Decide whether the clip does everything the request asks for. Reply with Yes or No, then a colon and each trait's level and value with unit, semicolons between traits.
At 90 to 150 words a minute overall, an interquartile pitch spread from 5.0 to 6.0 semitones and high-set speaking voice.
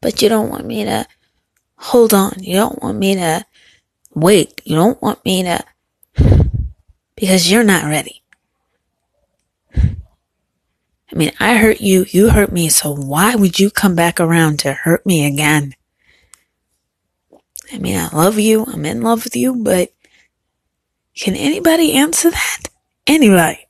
Yes: average, 145 wpm; wide, 5.6 semitones; high, 195 Hz